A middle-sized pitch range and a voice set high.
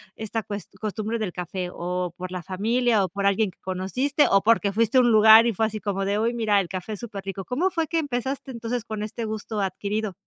Yes: average, 3.1 semitones; high, 215 Hz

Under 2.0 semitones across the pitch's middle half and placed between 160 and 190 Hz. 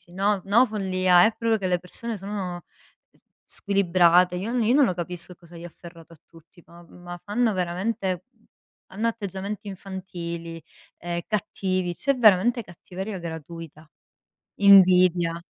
No: average, 2.8 semitones; medium, 185 Hz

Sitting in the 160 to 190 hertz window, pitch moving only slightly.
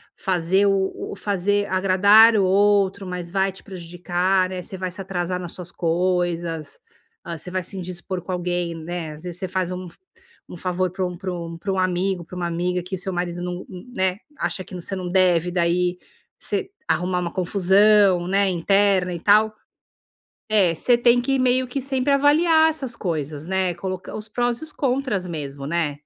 Yes: medium, 185 Hz; narrow, 2.3 semitones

